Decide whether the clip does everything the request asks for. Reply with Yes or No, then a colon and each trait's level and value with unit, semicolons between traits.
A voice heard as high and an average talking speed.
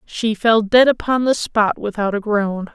Yes: high, 215 Hz; average, 195 wpm